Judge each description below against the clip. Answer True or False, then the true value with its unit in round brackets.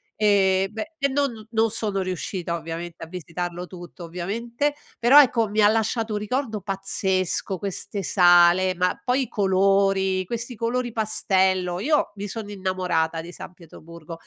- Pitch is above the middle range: True (195 Hz)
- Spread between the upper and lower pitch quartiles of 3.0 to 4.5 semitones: True (3.7 semitones)